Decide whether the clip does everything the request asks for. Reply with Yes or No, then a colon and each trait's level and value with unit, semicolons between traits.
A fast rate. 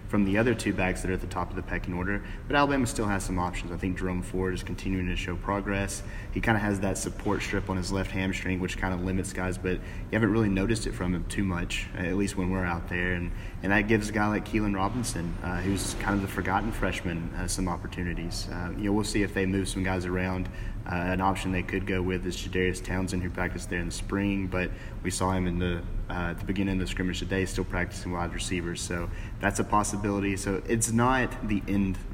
Yes: fast, 250 wpm